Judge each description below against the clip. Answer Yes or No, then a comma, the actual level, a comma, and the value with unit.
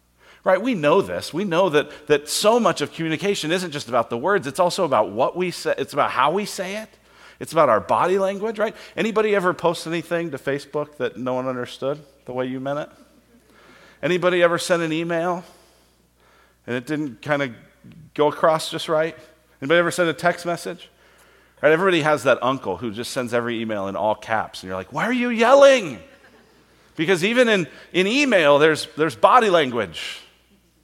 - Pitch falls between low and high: Yes, medium, 160 Hz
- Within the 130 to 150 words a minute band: No, average, 195 wpm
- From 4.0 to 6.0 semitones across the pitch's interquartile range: Yes, wide, 5.6 semitones